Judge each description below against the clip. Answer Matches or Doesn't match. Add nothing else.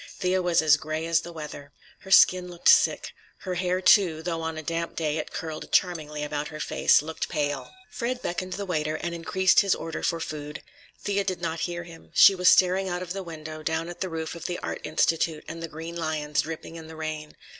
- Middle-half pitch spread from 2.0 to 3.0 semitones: Matches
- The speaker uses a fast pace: Matches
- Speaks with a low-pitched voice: Doesn't match